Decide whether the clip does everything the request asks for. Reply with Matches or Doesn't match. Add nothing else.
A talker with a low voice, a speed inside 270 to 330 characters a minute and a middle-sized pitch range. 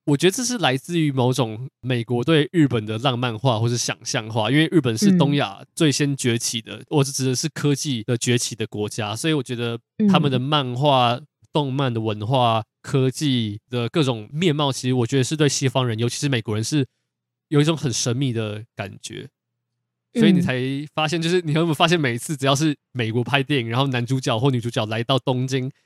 Matches